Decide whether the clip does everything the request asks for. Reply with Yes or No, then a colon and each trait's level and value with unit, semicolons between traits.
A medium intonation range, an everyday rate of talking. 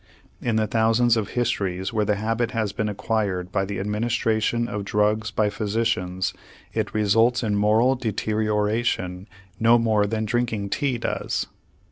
No: narrow, 2.0 semitones; average, 145 wpm